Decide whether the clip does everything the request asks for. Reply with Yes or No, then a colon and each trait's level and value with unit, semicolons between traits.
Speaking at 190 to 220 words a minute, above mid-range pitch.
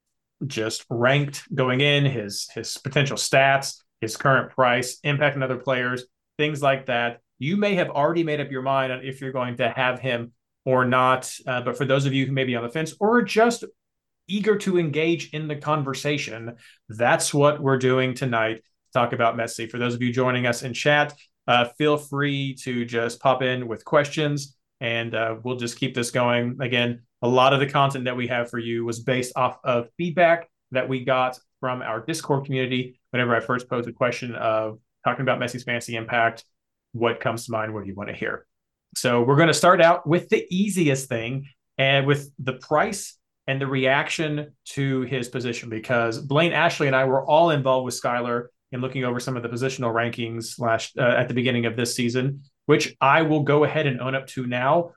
No: fast, 205 wpm; low, 130 Hz